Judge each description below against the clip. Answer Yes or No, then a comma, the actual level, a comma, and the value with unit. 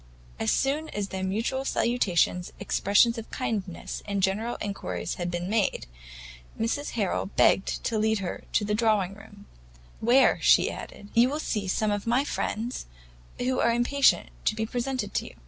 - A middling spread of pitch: Yes, average, 3.3 semitones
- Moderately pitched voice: No, high, 220 Hz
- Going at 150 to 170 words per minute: Yes, average, 165 wpm